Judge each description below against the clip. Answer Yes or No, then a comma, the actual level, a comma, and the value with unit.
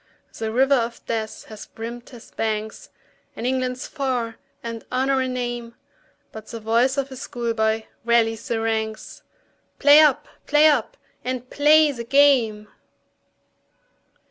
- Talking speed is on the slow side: Yes, slow, 130 wpm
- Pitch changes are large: No, average, 2.8 semitones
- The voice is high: Yes, high, 240 Hz